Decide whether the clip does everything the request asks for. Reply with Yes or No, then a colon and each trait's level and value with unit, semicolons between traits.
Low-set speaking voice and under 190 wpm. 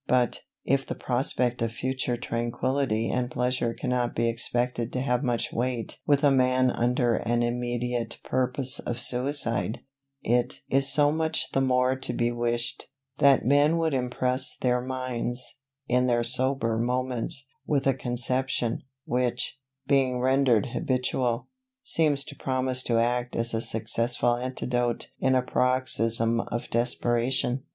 Yes: low, 125 Hz; average, 140 wpm